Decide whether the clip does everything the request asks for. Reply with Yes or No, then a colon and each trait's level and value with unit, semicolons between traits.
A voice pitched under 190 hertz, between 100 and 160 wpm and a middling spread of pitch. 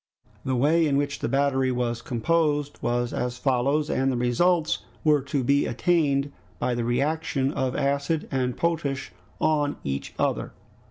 Yes: medium, 140 Hz; average, 155 wpm; average, 3.2 semitones